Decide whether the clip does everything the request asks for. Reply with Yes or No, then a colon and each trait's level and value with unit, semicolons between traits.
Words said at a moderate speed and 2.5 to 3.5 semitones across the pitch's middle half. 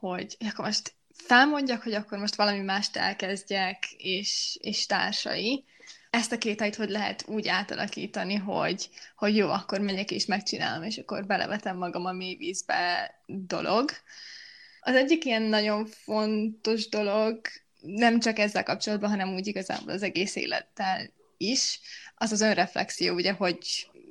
Yes: average, 145 wpm; average, 2.8 semitones